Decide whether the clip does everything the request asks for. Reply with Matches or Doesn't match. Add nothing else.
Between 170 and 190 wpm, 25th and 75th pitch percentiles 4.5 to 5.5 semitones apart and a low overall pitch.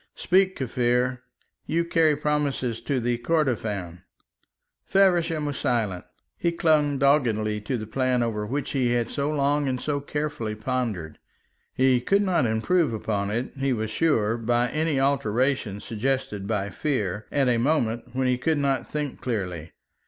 Doesn't match